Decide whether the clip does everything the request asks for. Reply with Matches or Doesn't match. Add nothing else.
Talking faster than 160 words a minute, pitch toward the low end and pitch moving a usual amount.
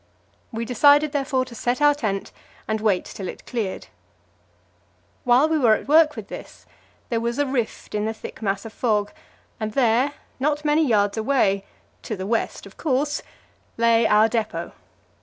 Doesn't match